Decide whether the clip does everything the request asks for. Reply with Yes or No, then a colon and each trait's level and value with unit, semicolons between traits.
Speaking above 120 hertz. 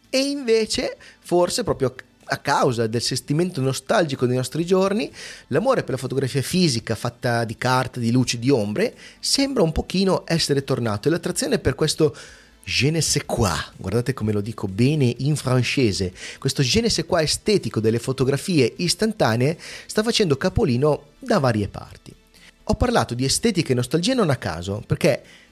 Yes: medium, 140 Hz